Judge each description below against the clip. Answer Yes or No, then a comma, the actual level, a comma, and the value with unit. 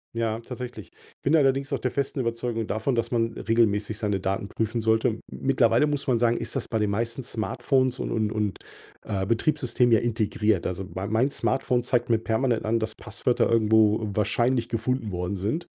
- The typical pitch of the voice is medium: No, low, 115 Hz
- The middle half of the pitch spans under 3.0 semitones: Yes, narrow, 2.4 semitones